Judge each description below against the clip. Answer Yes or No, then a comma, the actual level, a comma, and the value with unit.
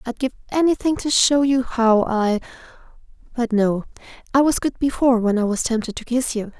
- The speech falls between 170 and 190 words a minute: Yes, average, 180 wpm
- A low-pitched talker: No, high, 245 Hz